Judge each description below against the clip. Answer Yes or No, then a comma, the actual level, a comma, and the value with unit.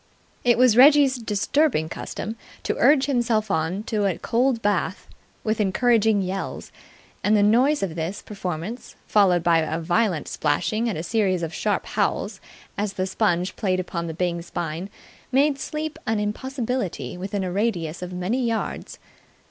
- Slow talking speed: No, average, 155 wpm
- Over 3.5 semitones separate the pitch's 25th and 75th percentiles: Yes, average, 4.9 semitones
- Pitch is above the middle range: Yes, high, 205 Hz